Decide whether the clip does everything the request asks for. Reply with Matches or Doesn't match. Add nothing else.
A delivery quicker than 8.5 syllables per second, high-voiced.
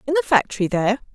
Matches